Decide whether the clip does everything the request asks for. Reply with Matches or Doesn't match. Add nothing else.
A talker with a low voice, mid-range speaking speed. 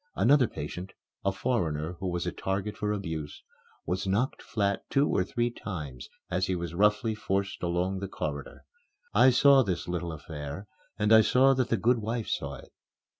Matches